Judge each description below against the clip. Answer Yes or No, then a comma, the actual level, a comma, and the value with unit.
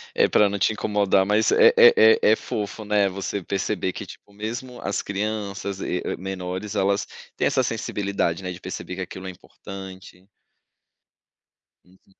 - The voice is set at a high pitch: No, low, 100 Hz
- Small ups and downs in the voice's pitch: Yes, narrow, 2.0 semitones